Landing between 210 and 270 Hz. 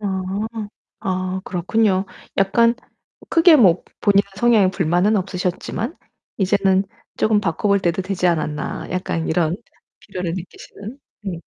No: high, 190 Hz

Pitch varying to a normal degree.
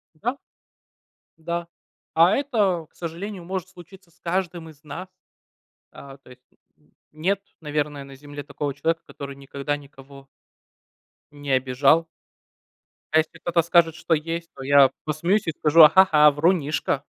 Yes: average, 3.3 semitones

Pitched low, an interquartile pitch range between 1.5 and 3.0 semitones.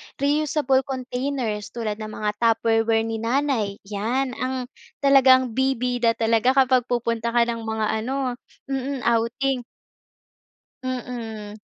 No: high, 245 Hz; average, 2.7 semitones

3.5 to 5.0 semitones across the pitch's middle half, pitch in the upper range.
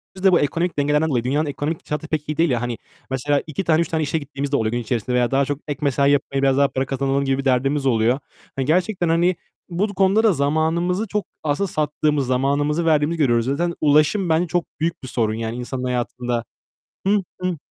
No: average, 3.9 semitones; medium, 145 Hz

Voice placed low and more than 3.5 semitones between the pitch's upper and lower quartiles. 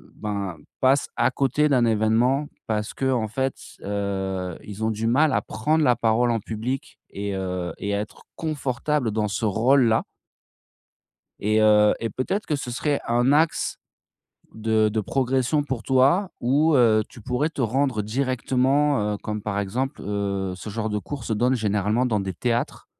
Yes: low, 115 Hz; average, 4.1 semitones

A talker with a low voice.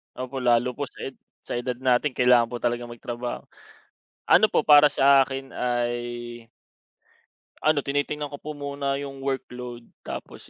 Yes: low, 130 Hz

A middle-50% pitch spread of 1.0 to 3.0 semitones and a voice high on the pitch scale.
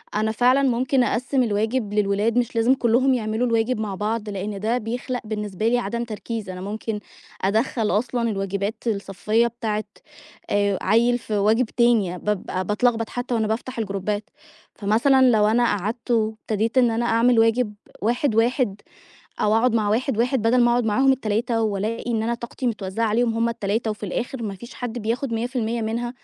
Yes: narrow, 2.4 semitones; high, 225 Hz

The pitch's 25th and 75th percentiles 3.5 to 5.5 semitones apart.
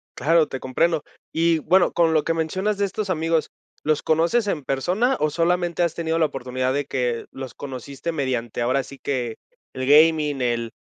Yes: average, 4.3 semitones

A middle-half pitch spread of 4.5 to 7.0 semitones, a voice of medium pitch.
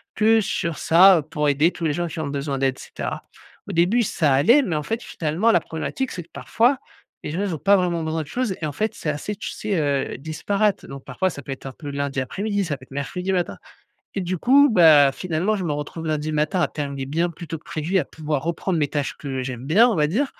Yes: average, 4.8 semitones; medium, 160 Hz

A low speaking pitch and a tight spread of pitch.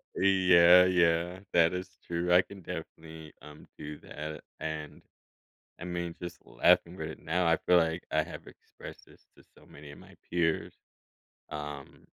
Yes: very low, 85 Hz; narrow, 2.1 semitones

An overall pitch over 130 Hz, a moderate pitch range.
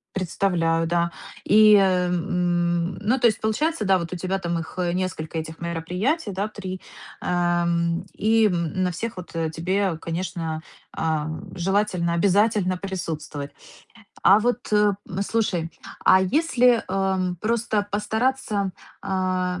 Yes: medium, 185 Hz; average, 3.4 semitones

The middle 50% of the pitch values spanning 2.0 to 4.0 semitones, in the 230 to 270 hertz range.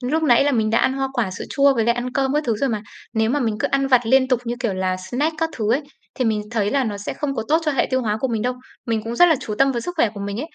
Yes: average, 3.7 semitones; high, 245 Hz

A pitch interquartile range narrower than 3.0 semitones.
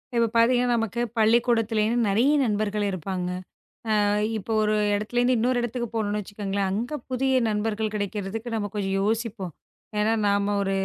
Yes: narrow, 2.4 semitones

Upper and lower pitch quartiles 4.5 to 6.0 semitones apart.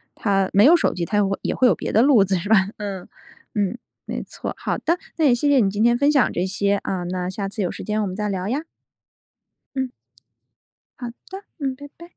Yes: average, 5.3 semitones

